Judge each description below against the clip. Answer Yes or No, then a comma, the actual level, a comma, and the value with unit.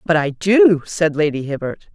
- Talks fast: No, average, 185 wpm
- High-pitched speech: No, medium, 155 Hz